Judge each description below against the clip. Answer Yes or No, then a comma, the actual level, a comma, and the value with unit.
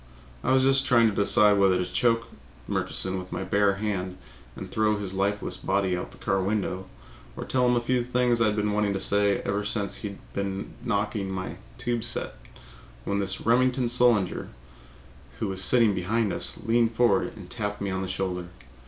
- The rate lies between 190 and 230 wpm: Yes, average, 195 wpm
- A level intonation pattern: No, average, 3.3 semitones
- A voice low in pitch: Yes, low, 105 Hz